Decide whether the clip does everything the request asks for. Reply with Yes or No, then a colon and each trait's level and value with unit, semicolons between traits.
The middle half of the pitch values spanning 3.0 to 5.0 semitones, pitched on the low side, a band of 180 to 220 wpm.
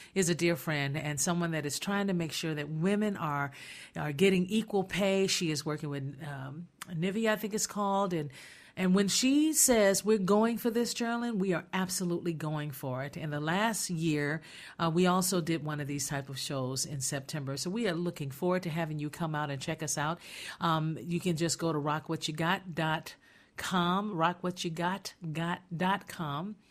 No: average, 4.1 semitones; medium, 170 Hz; average, 185 wpm